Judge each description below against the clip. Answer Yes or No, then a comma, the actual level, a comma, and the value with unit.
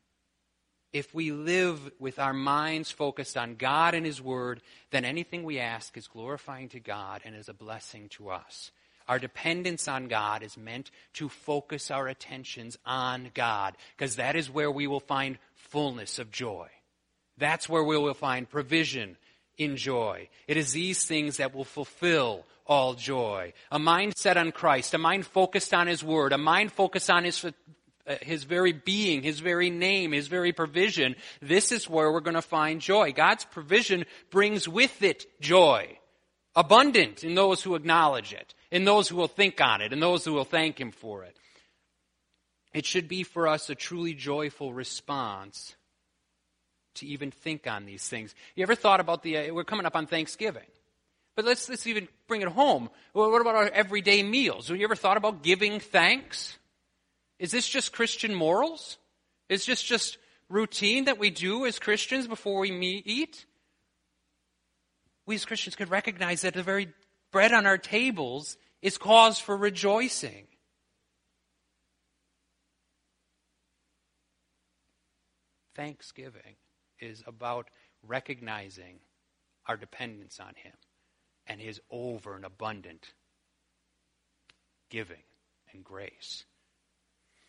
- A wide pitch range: Yes, wide, 7.7 semitones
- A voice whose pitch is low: No, medium, 155 Hz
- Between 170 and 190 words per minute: No, average, 150 wpm